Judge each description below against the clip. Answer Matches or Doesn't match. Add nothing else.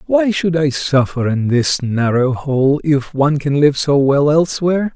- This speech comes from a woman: Doesn't match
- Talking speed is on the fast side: Doesn't match